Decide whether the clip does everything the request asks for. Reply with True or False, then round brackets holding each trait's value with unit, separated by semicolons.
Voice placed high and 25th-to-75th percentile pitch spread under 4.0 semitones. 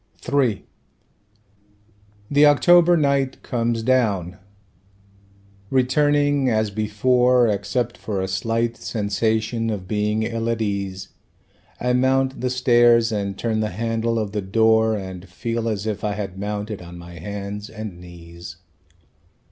False (110 Hz; 3.4 semitones)